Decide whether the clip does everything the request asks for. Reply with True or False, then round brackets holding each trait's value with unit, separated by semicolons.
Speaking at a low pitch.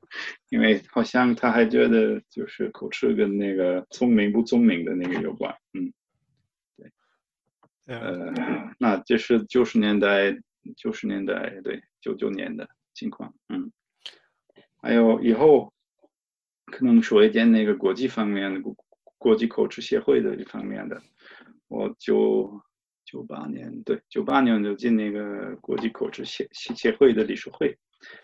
True (130 Hz)